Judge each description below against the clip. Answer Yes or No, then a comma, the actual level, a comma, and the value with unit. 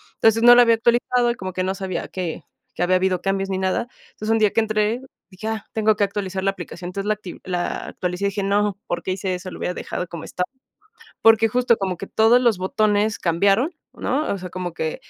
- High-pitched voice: Yes, high, 195 Hz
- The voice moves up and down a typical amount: Yes, average, 3.2 semitones